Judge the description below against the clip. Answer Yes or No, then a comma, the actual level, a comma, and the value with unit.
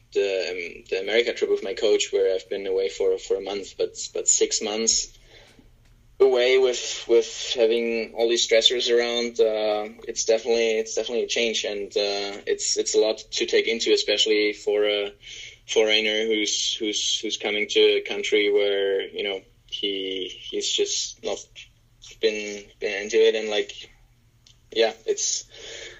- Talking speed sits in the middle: Yes, average, 160 wpm